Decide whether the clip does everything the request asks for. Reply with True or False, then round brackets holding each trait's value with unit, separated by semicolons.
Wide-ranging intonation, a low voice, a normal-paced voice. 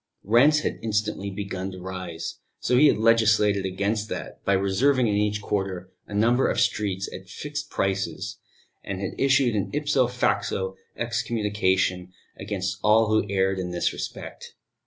False (3.2 semitones; 100 Hz; 155 wpm)